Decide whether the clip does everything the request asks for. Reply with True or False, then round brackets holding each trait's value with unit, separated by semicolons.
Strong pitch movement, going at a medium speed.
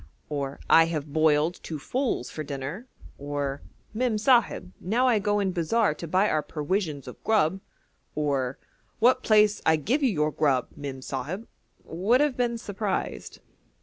True (6.7 semitones; 150 wpm)